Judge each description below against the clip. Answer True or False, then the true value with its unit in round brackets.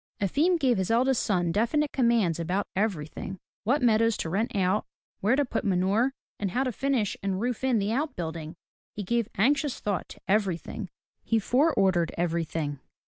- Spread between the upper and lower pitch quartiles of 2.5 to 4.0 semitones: False (5.2 semitones)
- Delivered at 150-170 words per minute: False (180 wpm)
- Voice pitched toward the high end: True (210 Hz)